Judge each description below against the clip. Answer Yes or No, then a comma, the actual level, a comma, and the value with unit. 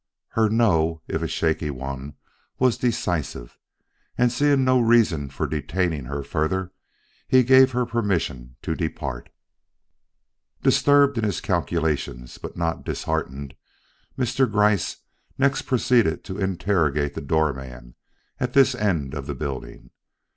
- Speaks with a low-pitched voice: Yes, very low, 85 Hz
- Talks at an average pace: No, slow, 130 wpm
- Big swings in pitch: Yes, wide, 8.8 semitones